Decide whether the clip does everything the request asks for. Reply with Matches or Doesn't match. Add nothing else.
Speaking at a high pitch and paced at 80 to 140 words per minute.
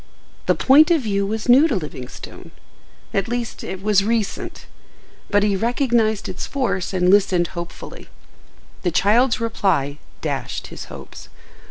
Matches